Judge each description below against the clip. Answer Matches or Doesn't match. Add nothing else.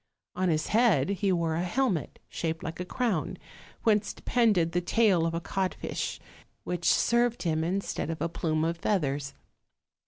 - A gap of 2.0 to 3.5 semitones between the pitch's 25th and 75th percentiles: Doesn't match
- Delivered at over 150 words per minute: Matches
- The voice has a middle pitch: Matches